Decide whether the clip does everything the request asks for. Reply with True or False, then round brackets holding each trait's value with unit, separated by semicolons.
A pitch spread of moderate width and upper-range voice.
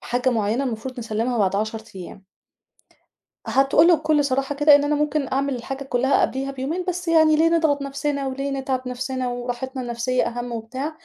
True (3.0 semitones; 265 Hz)